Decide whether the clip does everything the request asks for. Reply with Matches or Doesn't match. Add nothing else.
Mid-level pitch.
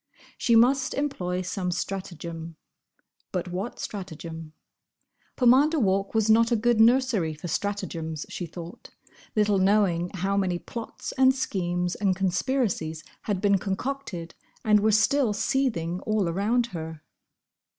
Doesn't match